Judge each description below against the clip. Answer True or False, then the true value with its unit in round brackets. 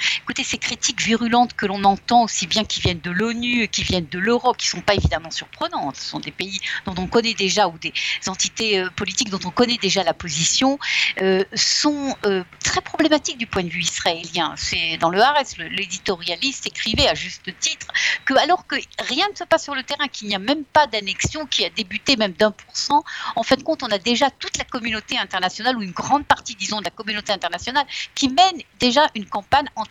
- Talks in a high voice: True (225 Hz)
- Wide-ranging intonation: True (6.3 semitones)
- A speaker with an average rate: False (225 wpm)